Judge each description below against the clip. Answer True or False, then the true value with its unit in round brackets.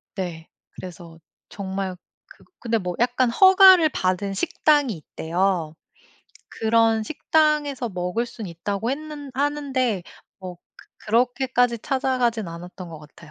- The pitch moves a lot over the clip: True (6.5 semitones)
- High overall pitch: True (225 Hz)